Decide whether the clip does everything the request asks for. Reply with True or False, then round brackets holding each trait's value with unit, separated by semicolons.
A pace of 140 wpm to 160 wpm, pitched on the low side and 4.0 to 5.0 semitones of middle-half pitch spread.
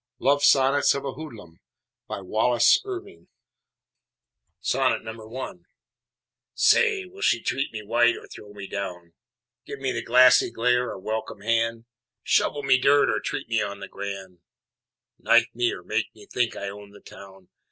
True (155 wpm; 115 Hz; 4.7 semitones)